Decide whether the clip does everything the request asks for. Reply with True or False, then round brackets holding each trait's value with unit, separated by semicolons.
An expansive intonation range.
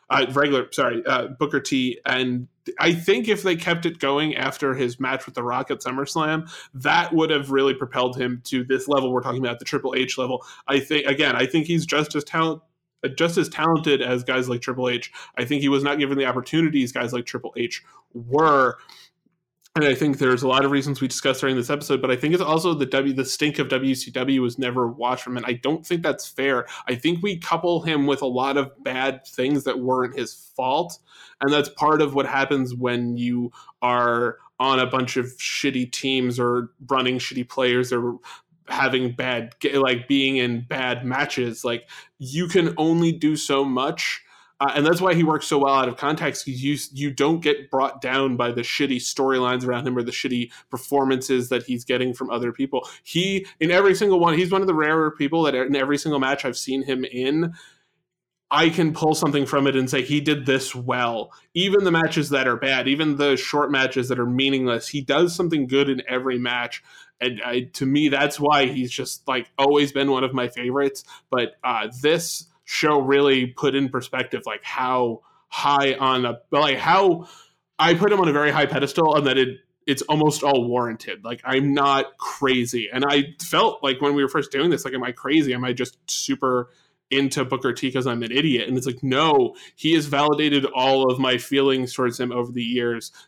False (2.8 semitones)